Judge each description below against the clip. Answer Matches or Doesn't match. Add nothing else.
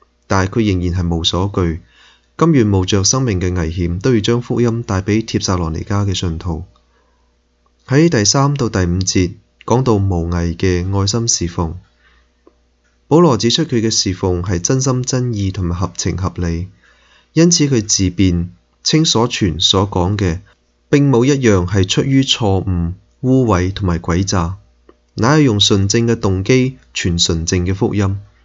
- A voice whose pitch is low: Matches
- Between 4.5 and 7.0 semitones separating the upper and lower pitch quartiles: Matches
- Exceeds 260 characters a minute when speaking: Doesn't match